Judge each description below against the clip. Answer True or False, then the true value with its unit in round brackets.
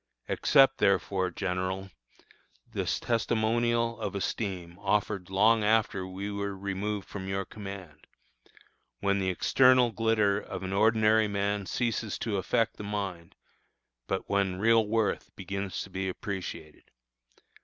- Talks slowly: True (125 wpm)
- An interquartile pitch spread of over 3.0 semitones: False (2.5 semitones)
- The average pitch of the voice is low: True (100 Hz)